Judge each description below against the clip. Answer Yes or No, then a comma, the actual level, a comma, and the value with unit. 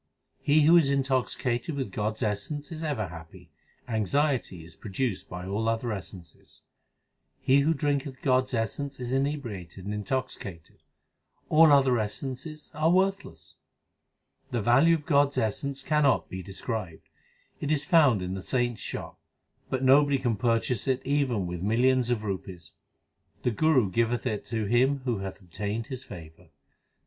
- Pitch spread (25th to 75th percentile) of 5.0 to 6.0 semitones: Yes, wide, 5.4 semitones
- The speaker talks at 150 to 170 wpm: Yes, average, 155 wpm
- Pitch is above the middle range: No, low, 125 Hz